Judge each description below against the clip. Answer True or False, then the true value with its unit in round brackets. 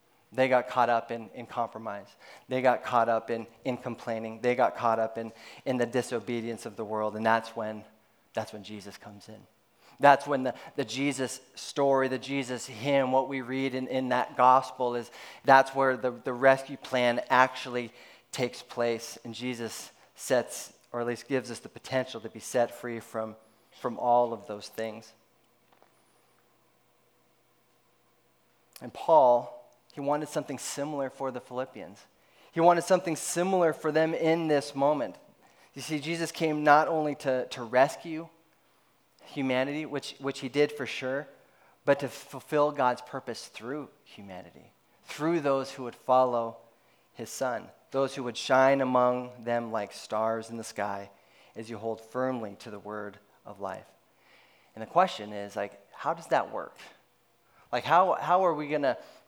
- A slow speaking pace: False (165 wpm)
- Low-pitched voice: True (125 Hz)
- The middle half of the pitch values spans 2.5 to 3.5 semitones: True (3.2 semitones)